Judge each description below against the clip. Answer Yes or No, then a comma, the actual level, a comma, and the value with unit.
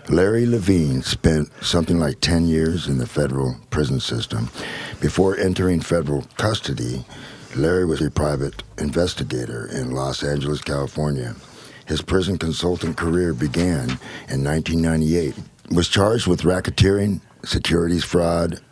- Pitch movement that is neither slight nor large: Yes, average, 3.5 semitones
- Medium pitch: No, very low, 85 Hz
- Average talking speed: No, slow, 130 wpm